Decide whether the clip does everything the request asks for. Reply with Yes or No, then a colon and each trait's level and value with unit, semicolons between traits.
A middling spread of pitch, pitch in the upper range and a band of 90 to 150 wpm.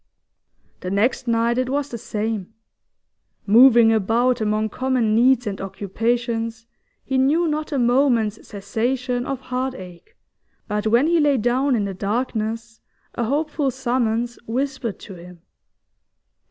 Yes: average, 3.2 semitones; high, 235 Hz; slow, 135 wpm